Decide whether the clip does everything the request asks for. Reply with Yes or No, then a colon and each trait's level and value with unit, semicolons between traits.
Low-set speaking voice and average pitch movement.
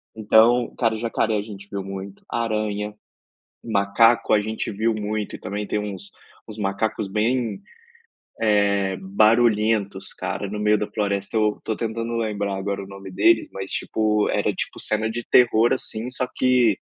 No: low, 105 Hz; narrow, 2.1 semitones